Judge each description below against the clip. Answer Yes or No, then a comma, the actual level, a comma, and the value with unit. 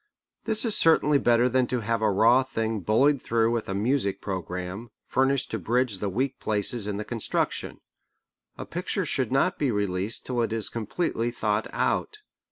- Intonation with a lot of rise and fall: No, average, 3.8 semitones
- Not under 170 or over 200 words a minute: Yes, average, 175 wpm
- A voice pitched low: Yes, low, 115 Hz